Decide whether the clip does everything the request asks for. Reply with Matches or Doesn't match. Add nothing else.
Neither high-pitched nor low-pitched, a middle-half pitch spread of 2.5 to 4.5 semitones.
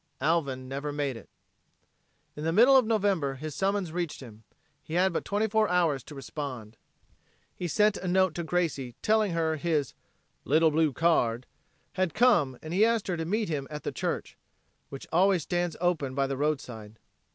Doesn't match